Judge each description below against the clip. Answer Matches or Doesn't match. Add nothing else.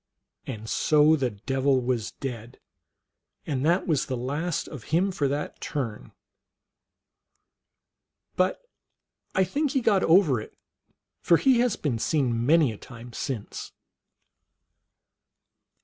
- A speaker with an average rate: Doesn't match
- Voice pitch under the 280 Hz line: Matches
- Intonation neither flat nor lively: Doesn't match